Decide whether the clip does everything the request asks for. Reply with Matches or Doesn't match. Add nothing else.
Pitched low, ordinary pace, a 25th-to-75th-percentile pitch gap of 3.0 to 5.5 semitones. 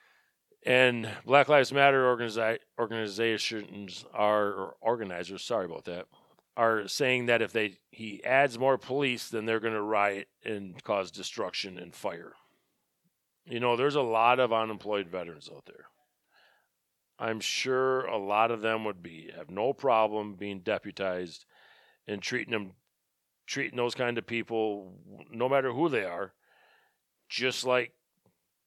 Matches